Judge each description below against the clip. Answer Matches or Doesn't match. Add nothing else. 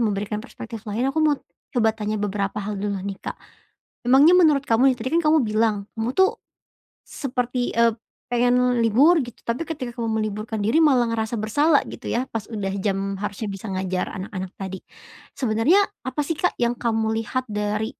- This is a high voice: Matches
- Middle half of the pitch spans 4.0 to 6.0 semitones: Doesn't match